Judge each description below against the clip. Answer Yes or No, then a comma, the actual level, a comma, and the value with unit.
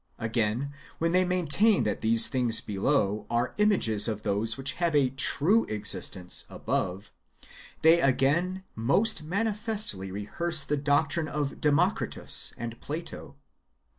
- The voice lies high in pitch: No, medium, 140 Hz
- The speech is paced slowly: Yes, slow, 125 wpm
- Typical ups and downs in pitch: No, wide, 7.4 semitones